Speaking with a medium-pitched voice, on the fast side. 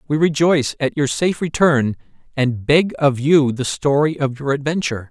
No: medium, 145 Hz; average, 175 wpm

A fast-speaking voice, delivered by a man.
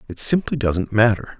No: average, 170 wpm; male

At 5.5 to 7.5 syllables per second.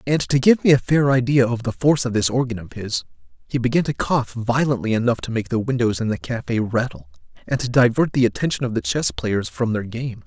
Yes: 5.7 syllables/s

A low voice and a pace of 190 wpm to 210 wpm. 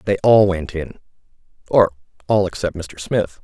No: very low, 95 Hz; average, 140 wpm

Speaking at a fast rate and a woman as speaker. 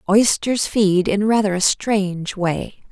No: average, 145 wpm; female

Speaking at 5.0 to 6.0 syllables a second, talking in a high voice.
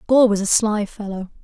Yes: 5.2 syllables/s; high, 210 Hz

